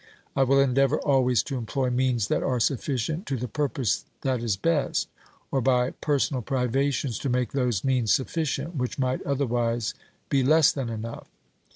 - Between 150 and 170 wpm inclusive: Yes, average, 165 wpm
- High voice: No, low, 130 Hz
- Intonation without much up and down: Yes, narrow, 2.1 semitones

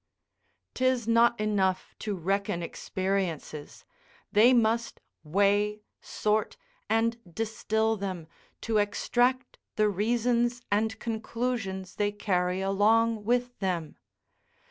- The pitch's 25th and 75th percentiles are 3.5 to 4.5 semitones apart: No, average, 3.0 semitones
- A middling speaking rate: No, slow, 100 wpm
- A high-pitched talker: Yes, high, 215 Hz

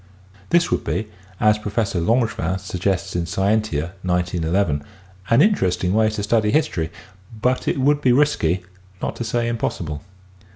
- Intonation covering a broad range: No, average, 4.7 semitones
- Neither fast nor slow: Yes, average, 150 wpm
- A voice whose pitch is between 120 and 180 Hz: No, low, 100 Hz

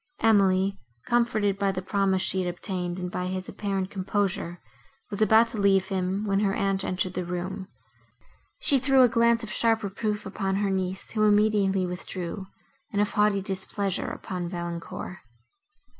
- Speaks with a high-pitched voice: Yes, high, 195 Hz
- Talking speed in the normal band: Yes, average, 160 wpm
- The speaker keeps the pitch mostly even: Yes, narrow, 2.0 semitones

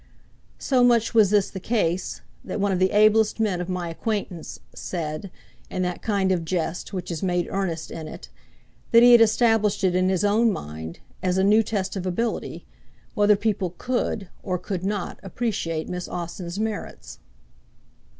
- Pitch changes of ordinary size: Yes, average, 3.2 semitones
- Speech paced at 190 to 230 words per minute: No, average, 175 wpm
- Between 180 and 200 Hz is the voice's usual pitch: Yes, high, 190 Hz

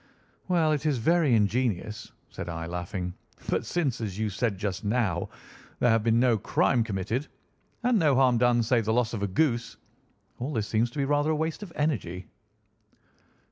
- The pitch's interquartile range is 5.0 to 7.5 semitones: Yes, average, 5.3 semitones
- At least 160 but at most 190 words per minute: Yes, average, 180 wpm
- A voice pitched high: No, low, 115 Hz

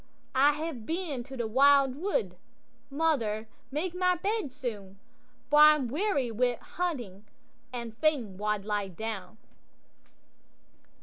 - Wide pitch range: Yes, wide, 6.0 semitones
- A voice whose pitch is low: No, very high, 265 Hz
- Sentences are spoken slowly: Yes, slow, 115 wpm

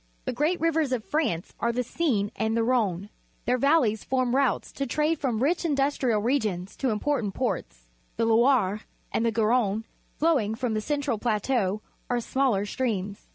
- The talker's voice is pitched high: Yes, high, 240 Hz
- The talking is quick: No, average, 165 wpm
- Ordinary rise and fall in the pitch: Yes, average, 4.5 semitones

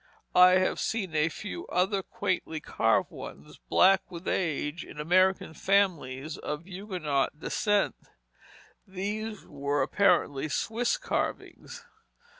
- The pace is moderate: No, slow, 110 wpm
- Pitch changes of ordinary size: Yes, average, 4.5 semitones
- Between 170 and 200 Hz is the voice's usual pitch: Yes, medium, 185 Hz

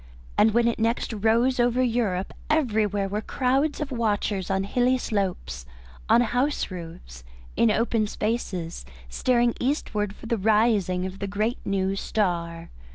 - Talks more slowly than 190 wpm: Yes, average, 145 wpm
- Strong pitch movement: No, average, 3.8 semitones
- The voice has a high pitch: Yes, high, 215 Hz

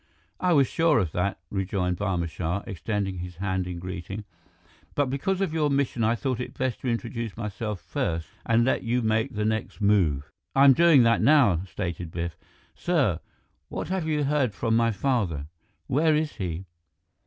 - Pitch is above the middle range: No, low, 110 Hz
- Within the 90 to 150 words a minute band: No, average, 175 wpm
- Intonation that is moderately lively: No, wide, 6.7 semitones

